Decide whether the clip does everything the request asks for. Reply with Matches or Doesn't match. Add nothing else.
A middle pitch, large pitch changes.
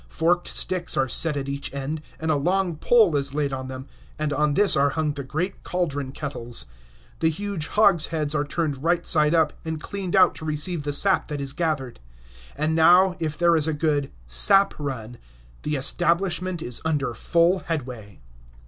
Doesn't match